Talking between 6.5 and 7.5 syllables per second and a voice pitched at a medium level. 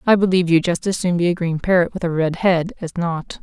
No: 6.0 syllables/s; medium, 175 Hz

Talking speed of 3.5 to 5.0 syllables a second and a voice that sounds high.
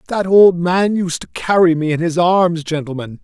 No: 4.6 syllables/s; medium, 170 Hz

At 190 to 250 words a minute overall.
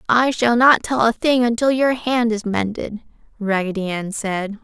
No: average, 180 wpm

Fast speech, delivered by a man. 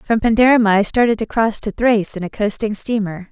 No: fast, 215 wpm; female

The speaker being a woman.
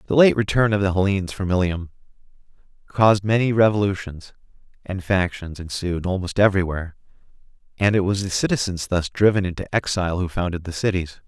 No: male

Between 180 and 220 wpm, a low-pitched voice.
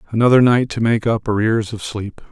Yes: fast, 205 wpm; low, 110 Hz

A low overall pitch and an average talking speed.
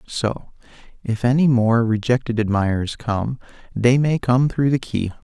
Yes: low, 120 Hz; average, 145 wpm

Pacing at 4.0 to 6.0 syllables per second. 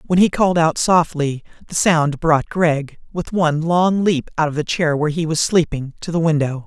Yes: 5.0 syllables/s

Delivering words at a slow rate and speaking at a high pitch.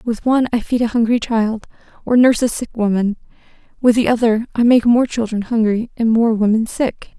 No: average, 200 wpm; high, 230 Hz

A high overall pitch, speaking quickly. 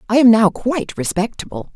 No: high, 215 Hz; average, 170 wpm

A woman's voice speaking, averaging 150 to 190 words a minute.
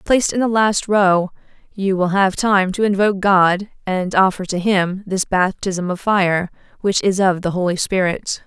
Yes: female; average, 185 wpm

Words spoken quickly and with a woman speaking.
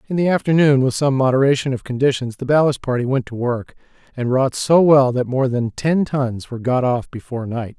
No: fast, 215 wpm; male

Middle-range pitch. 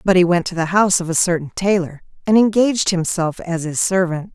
Yes: medium, 180 Hz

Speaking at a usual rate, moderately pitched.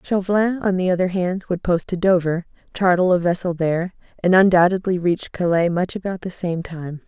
Yes: average, 185 wpm; medium, 180 Hz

